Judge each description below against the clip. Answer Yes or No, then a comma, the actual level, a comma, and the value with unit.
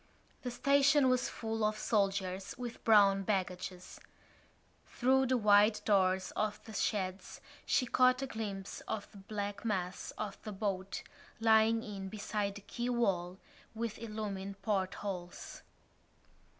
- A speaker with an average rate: No, slow, 130 wpm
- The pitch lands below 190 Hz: No, high, 210 Hz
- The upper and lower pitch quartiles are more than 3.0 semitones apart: No, average, 2.7 semitones